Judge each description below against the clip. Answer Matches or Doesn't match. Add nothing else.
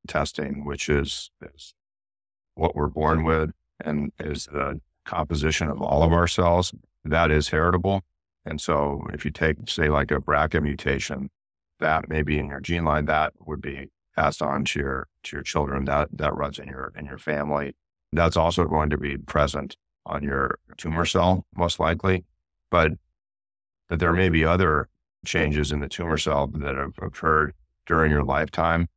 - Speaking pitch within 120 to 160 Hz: Doesn't match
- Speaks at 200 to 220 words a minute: Doesn't match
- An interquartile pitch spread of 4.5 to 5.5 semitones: Doesn't match